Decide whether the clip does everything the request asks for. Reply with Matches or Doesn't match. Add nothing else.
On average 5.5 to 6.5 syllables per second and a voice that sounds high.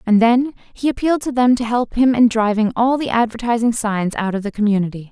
Matches